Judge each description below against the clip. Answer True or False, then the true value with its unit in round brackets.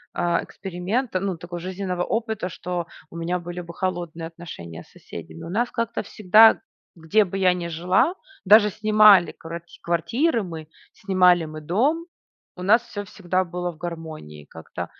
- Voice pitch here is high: False (180 Hz)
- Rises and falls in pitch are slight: False (3.5 semitones)